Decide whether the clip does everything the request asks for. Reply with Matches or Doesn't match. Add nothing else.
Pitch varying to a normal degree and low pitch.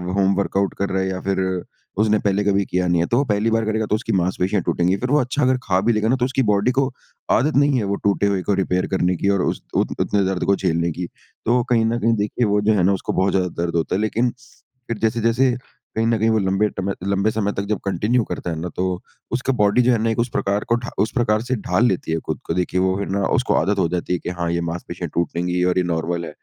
Matches